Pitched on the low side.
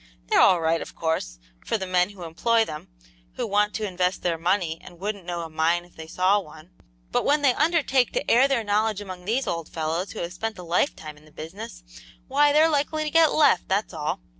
No: medium, 185 Hz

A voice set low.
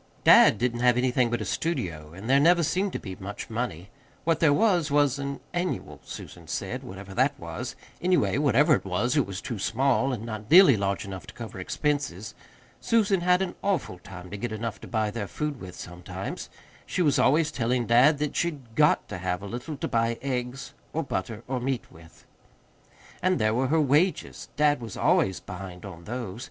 Yes: low, 125 Hz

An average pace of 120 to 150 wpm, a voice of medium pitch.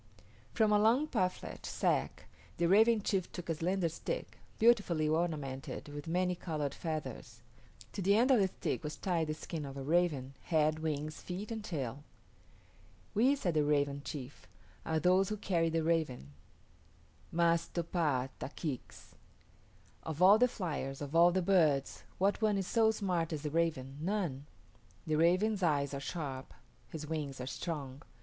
No: average, 165 wpm; medium, 165 Hz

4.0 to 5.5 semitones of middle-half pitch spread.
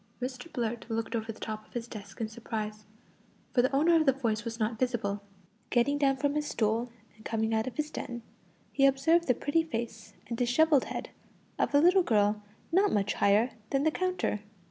Yes: average, 4.5 semitones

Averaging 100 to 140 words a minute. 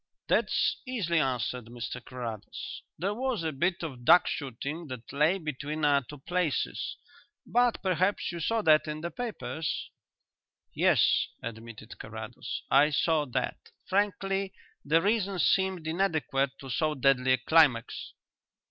Yes: slow, 135 wpm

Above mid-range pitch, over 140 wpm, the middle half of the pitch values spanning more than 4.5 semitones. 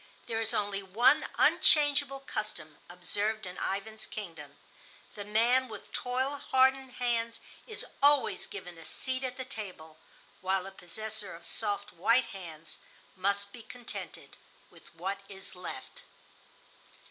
No: high, 215 Hz; slow, 135 wpm; average, 5.0 semitones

